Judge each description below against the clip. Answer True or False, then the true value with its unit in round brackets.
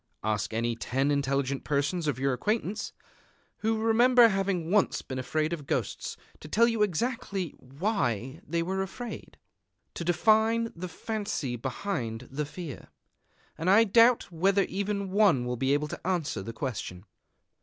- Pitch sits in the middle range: True (170 Hz)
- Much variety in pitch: True (7.5 semitones)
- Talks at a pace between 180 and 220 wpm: False (150 wpm)